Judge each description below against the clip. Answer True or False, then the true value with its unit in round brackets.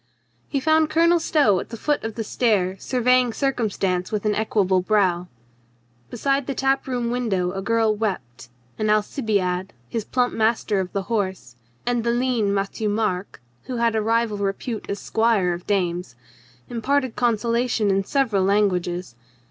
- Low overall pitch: False (220 Hz)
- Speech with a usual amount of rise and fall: True (4.0 semitones)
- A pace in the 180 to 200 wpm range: False (155 wpm)